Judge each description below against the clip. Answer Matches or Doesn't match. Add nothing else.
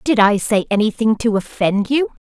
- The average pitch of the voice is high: Matches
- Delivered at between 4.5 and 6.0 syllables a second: Matches